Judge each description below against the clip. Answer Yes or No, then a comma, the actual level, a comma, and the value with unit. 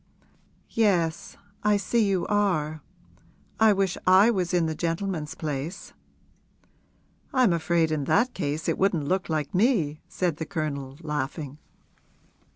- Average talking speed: No, slow, 130 wpm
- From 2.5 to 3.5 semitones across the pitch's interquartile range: No, average, 4.3 semitones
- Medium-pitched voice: Yes, medium, 170 Hz